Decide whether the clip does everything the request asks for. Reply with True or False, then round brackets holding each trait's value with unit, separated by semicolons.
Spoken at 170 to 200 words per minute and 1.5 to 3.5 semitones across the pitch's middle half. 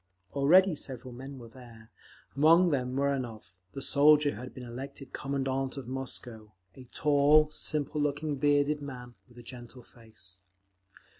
False (140 wpm; 3.0 semitones)